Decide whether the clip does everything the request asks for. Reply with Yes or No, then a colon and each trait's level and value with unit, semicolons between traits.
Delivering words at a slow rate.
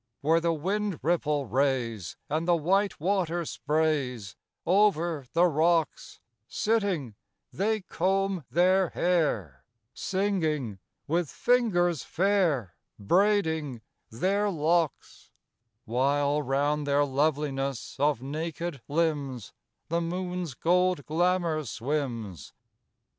Yes: slow, 95 wpm